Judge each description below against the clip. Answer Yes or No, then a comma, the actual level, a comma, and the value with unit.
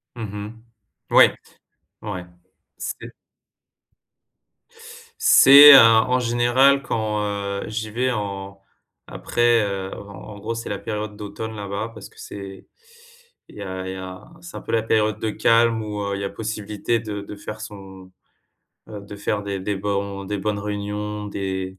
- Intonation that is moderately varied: No, narrow, 2.0 semitones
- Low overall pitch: Yes, low, 105 Hz